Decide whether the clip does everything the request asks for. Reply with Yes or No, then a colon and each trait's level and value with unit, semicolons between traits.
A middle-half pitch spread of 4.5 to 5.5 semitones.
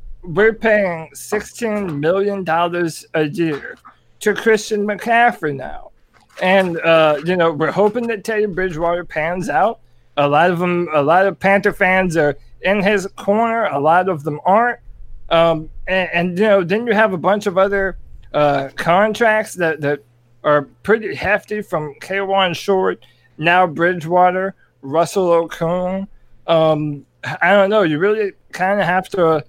No: average, 4.1 semitones